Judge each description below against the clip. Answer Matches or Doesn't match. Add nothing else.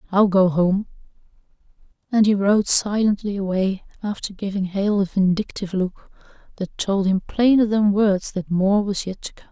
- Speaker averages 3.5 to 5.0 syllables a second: Matches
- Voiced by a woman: Matches